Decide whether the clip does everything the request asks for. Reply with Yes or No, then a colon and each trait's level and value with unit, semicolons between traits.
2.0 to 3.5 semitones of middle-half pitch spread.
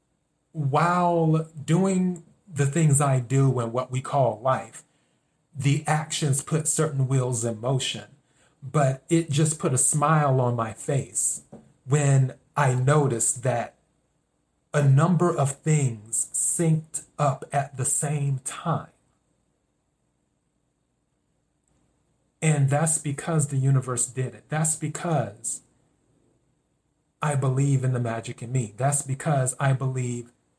Yes: average, 3.0 semitones